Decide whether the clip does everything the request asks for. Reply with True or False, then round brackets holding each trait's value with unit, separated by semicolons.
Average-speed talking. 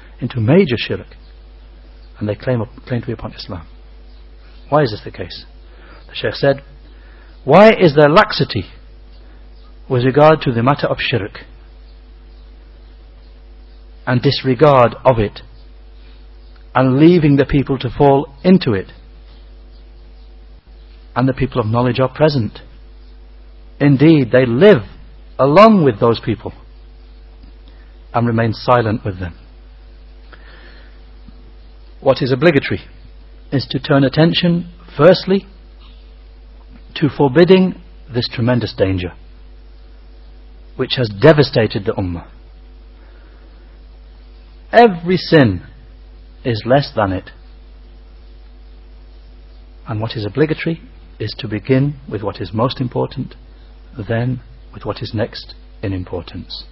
False (110 wpm)